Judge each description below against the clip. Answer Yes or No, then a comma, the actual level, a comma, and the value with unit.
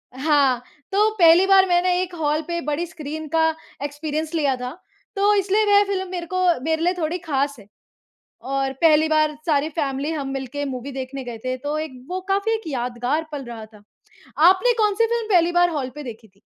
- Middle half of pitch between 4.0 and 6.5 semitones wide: Yes, average, 4.8 semitones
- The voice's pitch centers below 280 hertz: No, very high, 310 Hz